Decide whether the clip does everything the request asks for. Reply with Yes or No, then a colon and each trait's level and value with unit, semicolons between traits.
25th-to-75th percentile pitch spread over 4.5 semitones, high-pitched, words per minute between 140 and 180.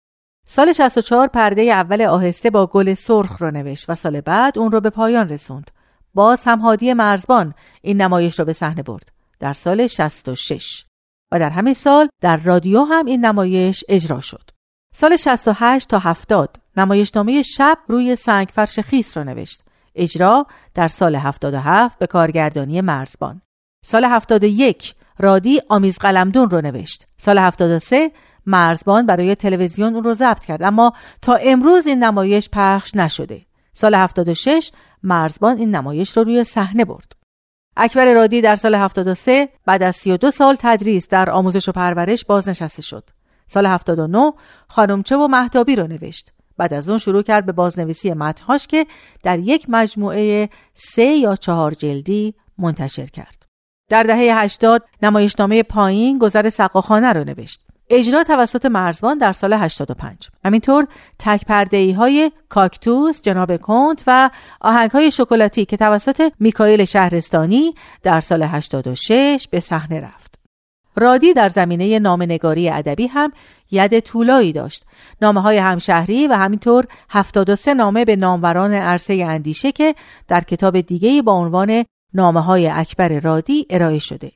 Yes: average, 5.0 semitones; high, 205 Hz; average, 145 wpm